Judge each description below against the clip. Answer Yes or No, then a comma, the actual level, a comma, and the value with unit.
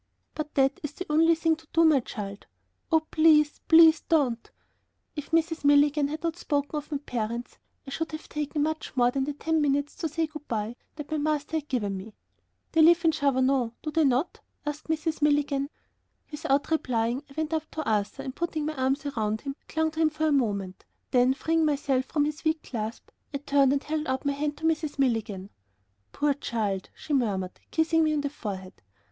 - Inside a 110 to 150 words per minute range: No, average, 200 wpm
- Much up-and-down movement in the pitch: No, average, 3.4 semitones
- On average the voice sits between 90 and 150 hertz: No, very high, 290 Hz